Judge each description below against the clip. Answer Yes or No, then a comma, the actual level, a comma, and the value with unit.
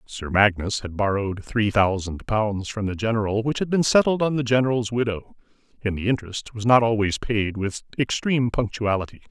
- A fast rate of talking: No, average, 180 wpm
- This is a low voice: Yes, low, 110 Hz